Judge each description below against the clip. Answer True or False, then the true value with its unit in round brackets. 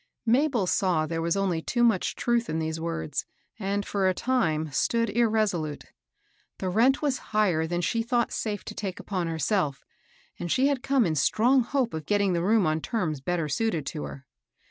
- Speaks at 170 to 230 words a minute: True (190 wpm)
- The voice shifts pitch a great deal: True (6.2 semitones)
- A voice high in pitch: True (195 Hz)